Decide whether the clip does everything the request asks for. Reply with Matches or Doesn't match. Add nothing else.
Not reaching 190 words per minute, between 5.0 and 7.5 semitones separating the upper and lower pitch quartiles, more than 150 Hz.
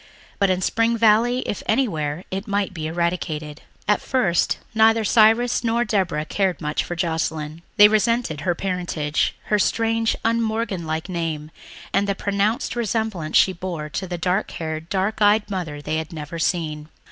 Matches